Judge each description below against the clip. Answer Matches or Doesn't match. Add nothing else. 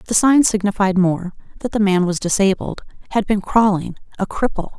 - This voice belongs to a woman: Matches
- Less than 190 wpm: Matches